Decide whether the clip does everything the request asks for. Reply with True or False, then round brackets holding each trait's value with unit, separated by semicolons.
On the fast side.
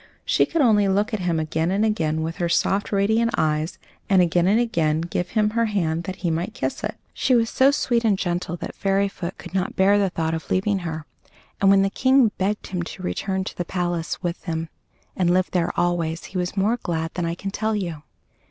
True (225 wpm)